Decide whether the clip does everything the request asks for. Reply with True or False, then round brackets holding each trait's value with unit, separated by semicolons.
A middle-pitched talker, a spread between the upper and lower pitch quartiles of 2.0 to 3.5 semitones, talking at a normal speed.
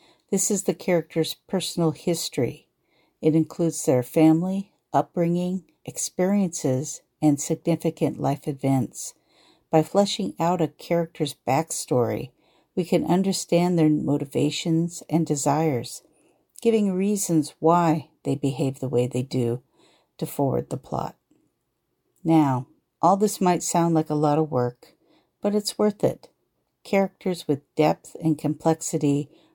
False (160 Hz; 3.0 semitones; 125 wpm)